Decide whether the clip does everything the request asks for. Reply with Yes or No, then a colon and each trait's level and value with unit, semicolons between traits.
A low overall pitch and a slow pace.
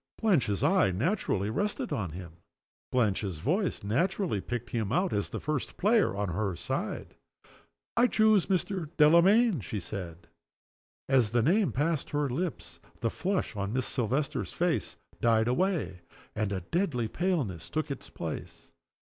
No: low, 130 Hz; average, 145 wpm